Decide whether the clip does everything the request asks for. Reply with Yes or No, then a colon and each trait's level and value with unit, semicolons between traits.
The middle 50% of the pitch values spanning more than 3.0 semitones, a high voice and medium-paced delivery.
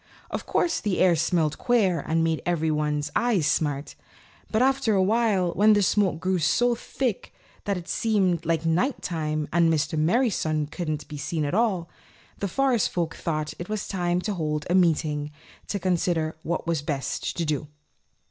No: average, 4.5 semitones; medium, 170 Hz; average, 175 wpm